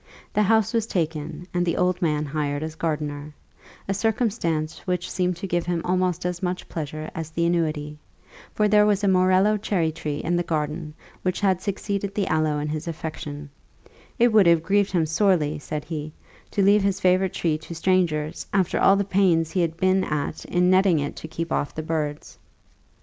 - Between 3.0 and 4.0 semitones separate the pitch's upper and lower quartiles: Yes, average, 3.6 semitones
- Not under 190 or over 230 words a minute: Yes, average, 195 wpm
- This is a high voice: No, medium, 175 Hz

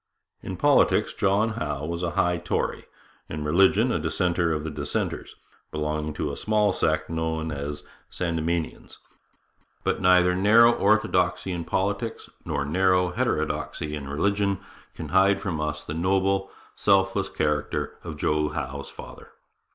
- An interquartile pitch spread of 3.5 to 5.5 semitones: Yes, average, 4.1 semitones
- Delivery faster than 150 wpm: No, average, 145 wpm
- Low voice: Yes, very low, 85 Hz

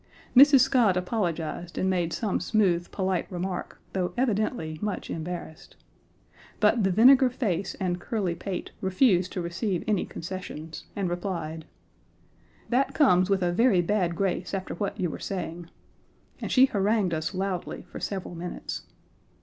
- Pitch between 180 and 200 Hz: Yes, medium, 185 Hz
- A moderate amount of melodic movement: Yes, average, 3.2 semitones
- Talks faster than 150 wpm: No, average, 145 wpm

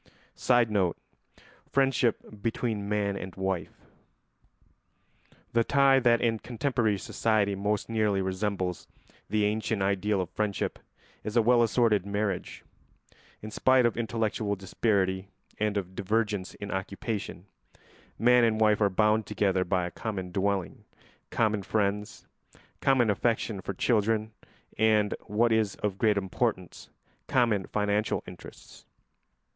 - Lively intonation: No, narrow, 2.4 semitones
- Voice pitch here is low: Yes, low, 105 Hz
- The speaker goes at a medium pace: No, slow, 120 wpm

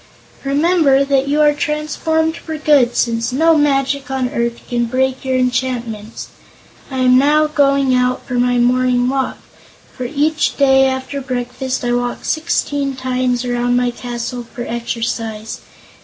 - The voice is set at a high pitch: Yes, very high, 260 Hz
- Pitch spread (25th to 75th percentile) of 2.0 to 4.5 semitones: Yes, narrow, 2.5 semitones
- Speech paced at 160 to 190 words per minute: No, average, 145 wpm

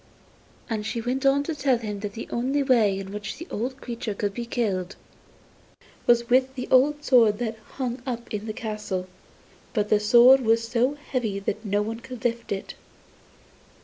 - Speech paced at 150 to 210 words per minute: Yes, average, 180 wpm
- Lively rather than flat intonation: No, average, 3.3 semitones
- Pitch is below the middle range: No, high, 230 Hz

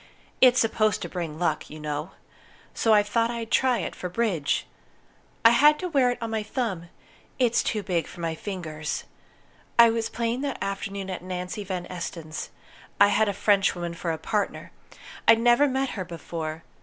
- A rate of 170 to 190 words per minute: Yes, average, 180 wpm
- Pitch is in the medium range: No, high, 200 Hz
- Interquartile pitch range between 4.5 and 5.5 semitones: Yes, average, 5.2 semitones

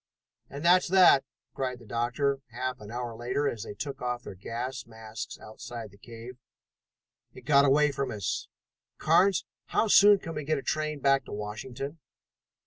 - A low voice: Yes, low, 130 Hz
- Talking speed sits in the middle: Yes, average, 170 wpm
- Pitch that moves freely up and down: No, average, 4.0 semitones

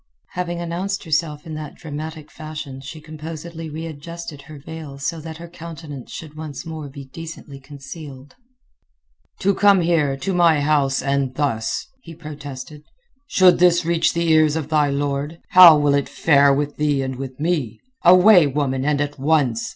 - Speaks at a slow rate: No, average, 165 wpm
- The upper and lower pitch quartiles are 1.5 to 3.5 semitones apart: Yes, average, 2.7 semitones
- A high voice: No, medium, 150 Hz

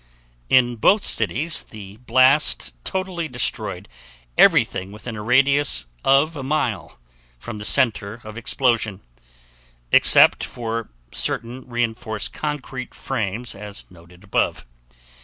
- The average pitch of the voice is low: Yes, low, 120 Hz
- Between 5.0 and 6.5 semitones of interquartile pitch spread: No, average, 4.1 semitones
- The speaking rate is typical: No, slow, 110 wpm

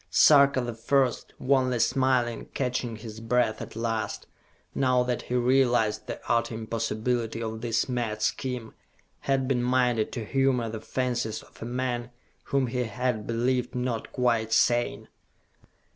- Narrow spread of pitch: Yes, narrow, 2.0 semitones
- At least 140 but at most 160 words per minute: Yes, average, 145 wpm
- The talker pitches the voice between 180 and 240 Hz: No, low, 120 Hz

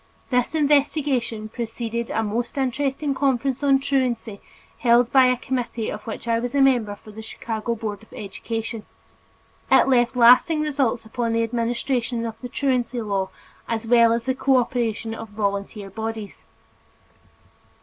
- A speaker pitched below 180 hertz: No, high, 235 Hz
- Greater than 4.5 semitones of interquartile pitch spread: No, average, 2.7 semitones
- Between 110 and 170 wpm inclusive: Yes, average, 150 wpm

